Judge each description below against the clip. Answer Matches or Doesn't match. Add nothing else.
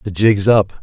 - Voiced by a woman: Doesn't match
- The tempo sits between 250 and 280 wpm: Doesn't match